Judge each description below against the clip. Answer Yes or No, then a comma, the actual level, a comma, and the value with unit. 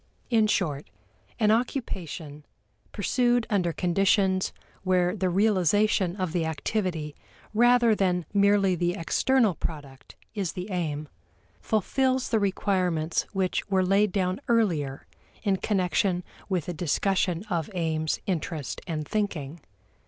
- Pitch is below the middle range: No, medium, 185 Hz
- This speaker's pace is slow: Yes, slow, 120 wpm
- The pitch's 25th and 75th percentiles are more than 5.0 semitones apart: No, average, 3.8 semitones